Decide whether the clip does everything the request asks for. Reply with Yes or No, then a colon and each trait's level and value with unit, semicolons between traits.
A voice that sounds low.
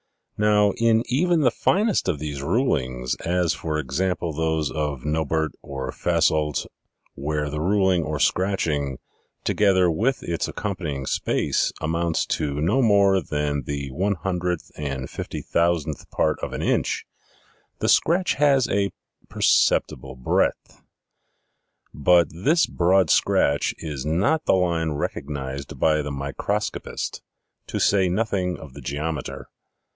Yes: very low, 80 Hz